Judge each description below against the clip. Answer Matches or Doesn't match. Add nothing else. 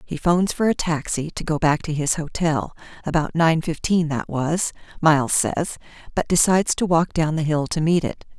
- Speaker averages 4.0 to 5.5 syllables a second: Matches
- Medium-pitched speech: Matches